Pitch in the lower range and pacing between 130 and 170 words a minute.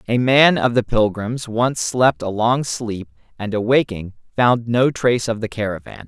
No: low, 115 Hz; average, 180 wpm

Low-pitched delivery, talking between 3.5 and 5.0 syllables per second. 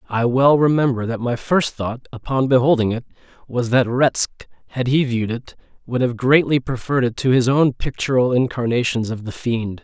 No: low, 125 Hz; 5.2 syllables/s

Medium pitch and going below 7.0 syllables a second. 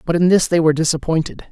No: medium, 165 Hz; 7.5 syllables/s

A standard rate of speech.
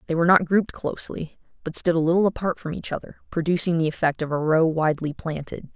No: fast, 220 wpm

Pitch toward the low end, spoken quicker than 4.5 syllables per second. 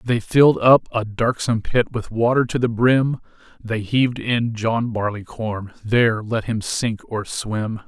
No: low, 115 Hz; 4.2 syllables/s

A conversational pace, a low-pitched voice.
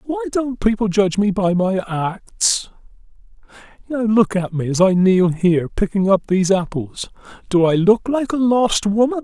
No: average, 170 wpm; high, 195 Hz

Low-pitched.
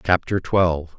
Yes: very low, 90 Hz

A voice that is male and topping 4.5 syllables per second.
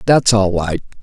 No: male; 4.4 syllables/s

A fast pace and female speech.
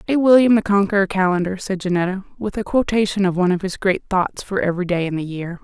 Yes: fast, 235 wpm; female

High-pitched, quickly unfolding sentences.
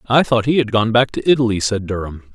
No: low, 115 Hz; fast, 255 wpm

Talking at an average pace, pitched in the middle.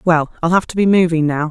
No: fast, 280 wpm; medium, 170 Hz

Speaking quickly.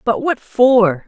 No: average, 165 wpm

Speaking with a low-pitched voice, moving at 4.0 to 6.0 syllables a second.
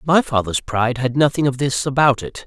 Yes: low, 130 Hz; 5.5 syllables/s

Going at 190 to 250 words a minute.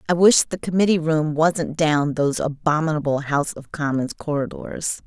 No: average, 155 wpm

